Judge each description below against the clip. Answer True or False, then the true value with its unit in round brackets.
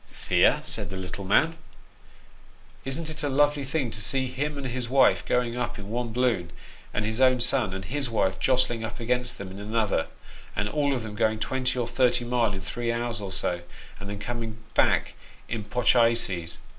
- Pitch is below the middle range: True (120 Hz)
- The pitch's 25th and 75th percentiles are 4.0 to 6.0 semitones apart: False (3.6 semitones)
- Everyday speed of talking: False (210 wpm)